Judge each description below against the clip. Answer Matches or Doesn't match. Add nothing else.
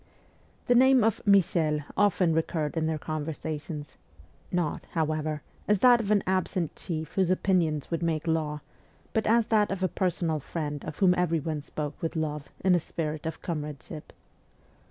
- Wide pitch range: Doesn't match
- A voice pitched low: Doesn't match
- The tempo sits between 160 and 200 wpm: Matches